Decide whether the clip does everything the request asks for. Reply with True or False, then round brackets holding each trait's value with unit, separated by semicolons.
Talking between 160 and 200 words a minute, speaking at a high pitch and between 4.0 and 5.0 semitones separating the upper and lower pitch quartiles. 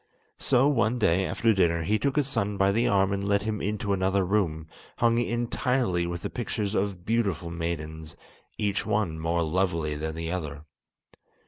False (175 wpm; 95 Hz; 4.5 semitones)